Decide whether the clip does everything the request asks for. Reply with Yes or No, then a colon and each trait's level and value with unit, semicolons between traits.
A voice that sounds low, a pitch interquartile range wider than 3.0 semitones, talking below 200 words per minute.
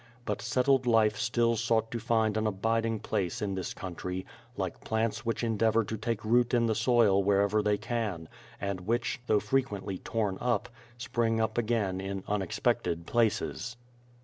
No: low, 110 Hz; average, 2.7 semitones; average, 160 wpm